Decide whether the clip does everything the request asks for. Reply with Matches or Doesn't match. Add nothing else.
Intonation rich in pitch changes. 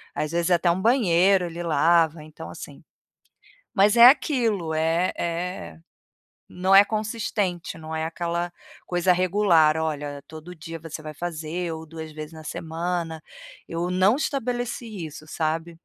Doesn't match